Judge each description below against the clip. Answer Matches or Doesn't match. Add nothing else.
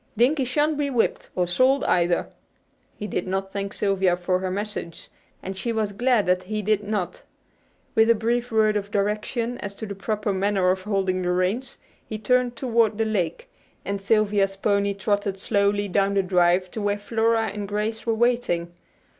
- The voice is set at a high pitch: Matches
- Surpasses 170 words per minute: Matches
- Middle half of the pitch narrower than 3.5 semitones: Matches